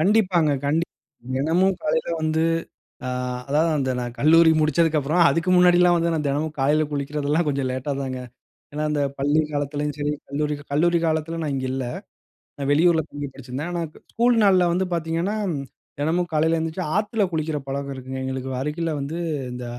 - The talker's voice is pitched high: No, medium, 155 Hz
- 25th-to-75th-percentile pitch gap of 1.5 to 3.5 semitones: Yes, average, 3.1 semitones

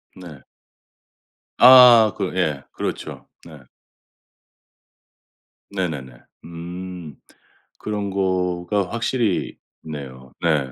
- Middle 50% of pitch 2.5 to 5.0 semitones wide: Yes, average, 4.6 semitones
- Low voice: Yes, very low, 90 Hz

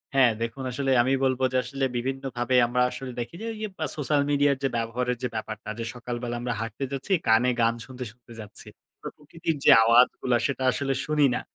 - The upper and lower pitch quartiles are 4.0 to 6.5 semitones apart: No, narrow, 2.4 semitones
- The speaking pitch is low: Yes, low, 125 Hz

